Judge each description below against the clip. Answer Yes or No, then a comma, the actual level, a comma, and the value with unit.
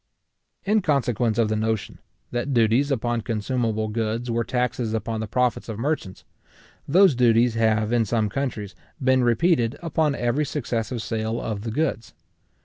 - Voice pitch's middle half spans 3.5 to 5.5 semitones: No, average, 2.7 semitones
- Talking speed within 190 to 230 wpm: No, average, 150 wpm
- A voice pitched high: No, low, 115 Hz